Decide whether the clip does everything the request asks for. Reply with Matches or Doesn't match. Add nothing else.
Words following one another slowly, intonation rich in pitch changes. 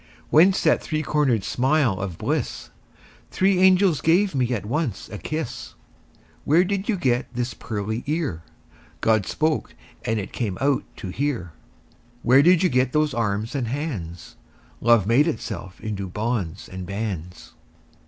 Doesn't match